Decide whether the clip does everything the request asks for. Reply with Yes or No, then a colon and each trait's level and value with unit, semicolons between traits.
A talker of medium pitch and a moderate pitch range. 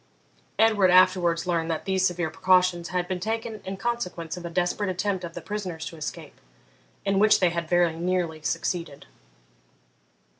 No: medium, 180 Hz; narrow, 2.1 semitones